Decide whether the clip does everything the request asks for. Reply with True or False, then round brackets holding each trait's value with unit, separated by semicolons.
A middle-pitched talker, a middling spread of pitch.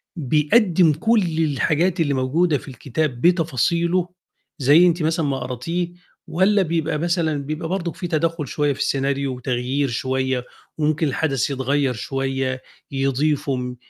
True (150 Hz; 4.0 semitones)